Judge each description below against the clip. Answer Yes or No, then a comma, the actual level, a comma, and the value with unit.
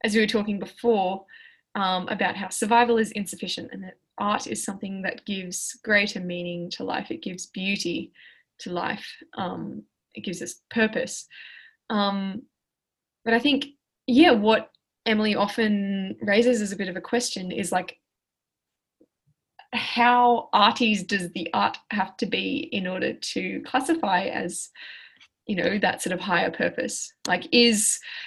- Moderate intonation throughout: Yes, average, 3.8 semitones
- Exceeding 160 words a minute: No, average, 150 wpm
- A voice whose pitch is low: No, high, 215 Hz